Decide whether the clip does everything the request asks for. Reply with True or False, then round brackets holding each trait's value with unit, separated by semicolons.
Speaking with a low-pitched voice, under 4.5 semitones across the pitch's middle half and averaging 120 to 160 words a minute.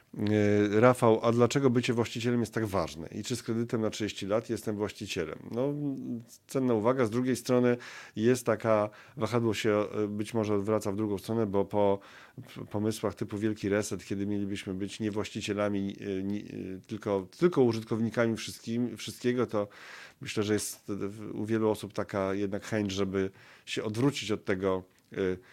True (105 Hz; 2.5 semitones; 150 wpm)